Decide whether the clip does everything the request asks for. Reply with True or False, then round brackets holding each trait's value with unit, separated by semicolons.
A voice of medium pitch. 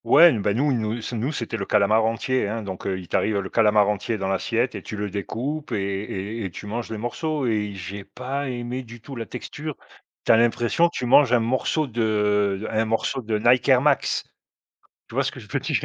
False (115 Hz)